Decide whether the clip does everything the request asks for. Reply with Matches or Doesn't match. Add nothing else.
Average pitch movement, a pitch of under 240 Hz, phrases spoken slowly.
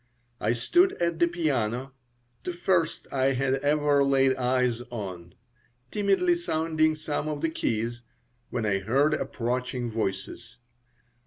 Matches